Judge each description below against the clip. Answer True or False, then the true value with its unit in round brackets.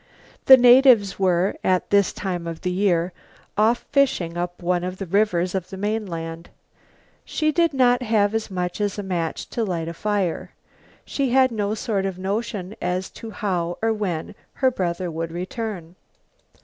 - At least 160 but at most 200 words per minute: True (170 wpm)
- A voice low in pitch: False (195 Hz)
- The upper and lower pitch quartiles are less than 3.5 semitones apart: False (3.9 semitones)